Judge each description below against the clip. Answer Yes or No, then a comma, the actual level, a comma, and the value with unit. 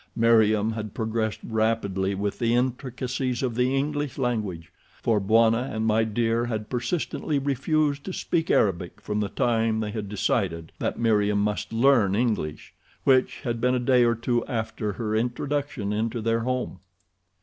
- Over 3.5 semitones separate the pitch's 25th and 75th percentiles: No, average, 2.9 semitones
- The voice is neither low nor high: No, low, 115 Hz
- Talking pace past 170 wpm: No, average, 160 wpm